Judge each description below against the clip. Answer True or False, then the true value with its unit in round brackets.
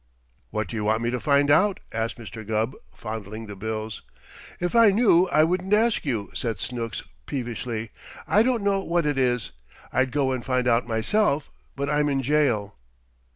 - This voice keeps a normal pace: True (180 wpm)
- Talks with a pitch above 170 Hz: False (125 Hz)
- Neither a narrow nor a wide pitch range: False (5.9 semitones)